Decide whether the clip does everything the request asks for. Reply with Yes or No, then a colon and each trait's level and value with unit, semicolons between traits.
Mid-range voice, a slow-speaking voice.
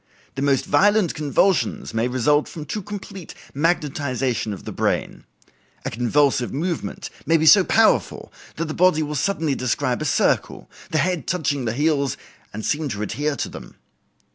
No: medium, 150 Hz; average, 165 wpm